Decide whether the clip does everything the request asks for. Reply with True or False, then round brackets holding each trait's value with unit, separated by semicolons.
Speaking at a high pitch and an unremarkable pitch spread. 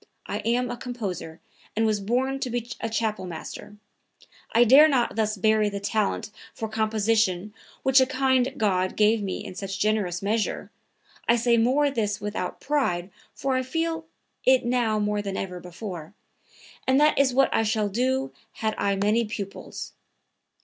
True (220 Hz; 3.7 semitones)